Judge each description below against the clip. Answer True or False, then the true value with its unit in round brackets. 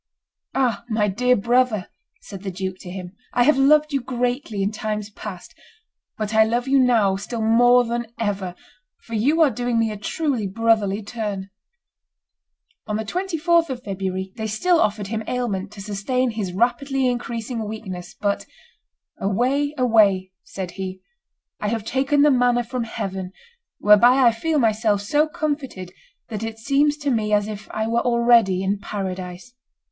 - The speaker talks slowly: False (160 wpm)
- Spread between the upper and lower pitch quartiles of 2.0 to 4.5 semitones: True (3.8 semitones)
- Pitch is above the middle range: True (225 Hz)